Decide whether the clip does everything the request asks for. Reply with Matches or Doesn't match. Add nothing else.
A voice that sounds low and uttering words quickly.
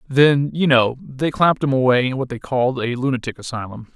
Matches